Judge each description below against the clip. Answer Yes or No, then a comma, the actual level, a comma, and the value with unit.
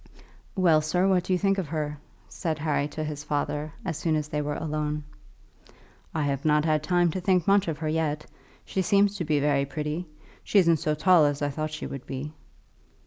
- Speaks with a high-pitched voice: No, medium, 155 Hz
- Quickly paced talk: Yes, fast, 210 wpm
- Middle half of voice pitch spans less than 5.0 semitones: Yes, average, 2.9 semitones